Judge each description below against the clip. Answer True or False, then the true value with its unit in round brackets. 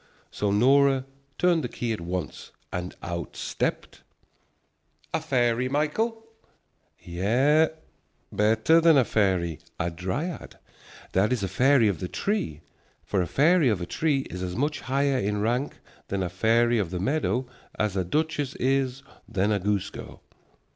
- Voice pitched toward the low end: True (115 Hz)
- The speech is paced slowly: False (155 wpm)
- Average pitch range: False (6.9 semitones)